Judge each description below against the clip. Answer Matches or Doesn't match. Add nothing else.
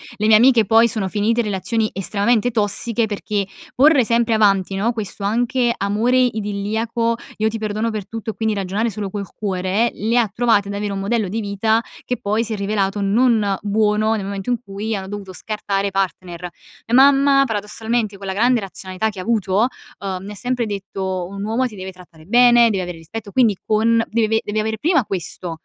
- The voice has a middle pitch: Doesn't match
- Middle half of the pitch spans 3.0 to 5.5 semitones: Doesn't match